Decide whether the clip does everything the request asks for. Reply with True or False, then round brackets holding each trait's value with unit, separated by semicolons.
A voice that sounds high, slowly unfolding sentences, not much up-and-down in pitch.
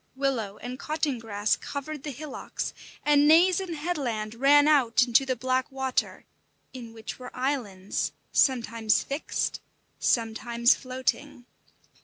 False (260 Hz; 125 wpm; 3.8 semitones)